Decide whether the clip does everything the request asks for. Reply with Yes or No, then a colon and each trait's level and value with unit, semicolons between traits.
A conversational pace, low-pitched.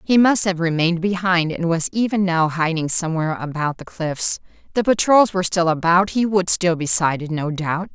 No: average, 195 wpm; medium, 175 Hz